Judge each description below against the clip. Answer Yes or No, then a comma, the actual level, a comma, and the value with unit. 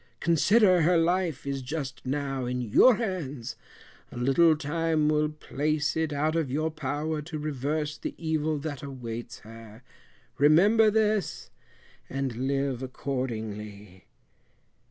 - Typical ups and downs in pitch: Yes, average, 3.6 semitones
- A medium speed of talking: No, slow, 125 wpm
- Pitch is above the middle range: No, medium, 150 Hz